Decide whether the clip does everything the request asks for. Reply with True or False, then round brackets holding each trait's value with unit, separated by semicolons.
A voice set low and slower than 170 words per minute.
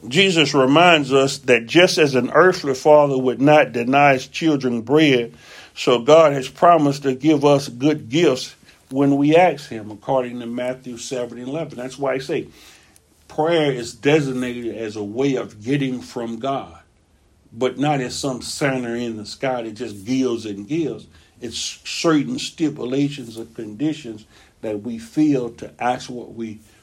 True (130 Hz; 160 wpm)